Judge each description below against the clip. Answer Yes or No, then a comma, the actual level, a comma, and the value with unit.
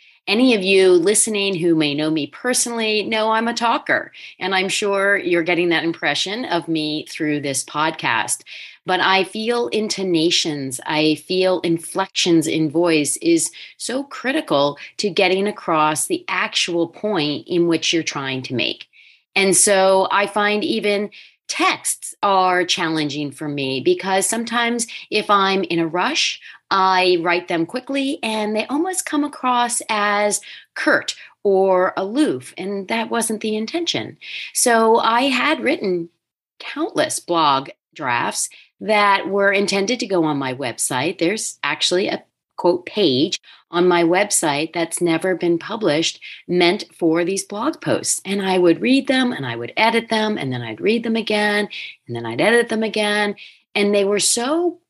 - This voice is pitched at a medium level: No, high, 195 Hz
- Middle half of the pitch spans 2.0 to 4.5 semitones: No, average, 4.9 semitones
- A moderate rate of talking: Yes, average, 155 wpm